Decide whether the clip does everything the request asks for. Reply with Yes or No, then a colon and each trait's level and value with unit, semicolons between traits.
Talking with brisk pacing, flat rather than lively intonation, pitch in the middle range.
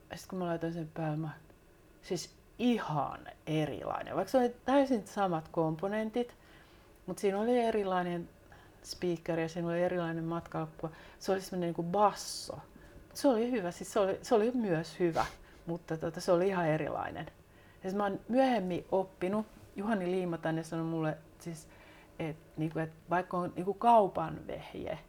No: fast, 160 wpm; average, 3.7 semitones; medium, 180 Hz